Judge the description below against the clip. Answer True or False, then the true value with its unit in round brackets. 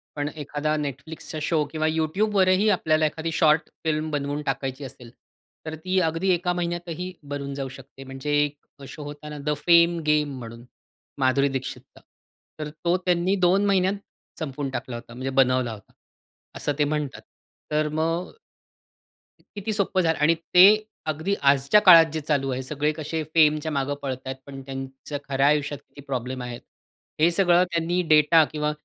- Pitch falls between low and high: True (150 Hz)